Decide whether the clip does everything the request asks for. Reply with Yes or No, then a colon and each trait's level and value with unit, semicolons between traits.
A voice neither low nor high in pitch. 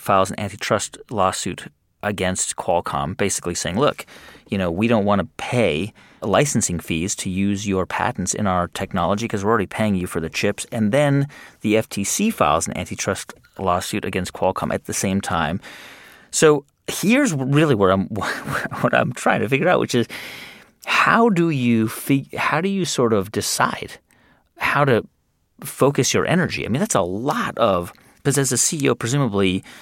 No: low, 110 Hz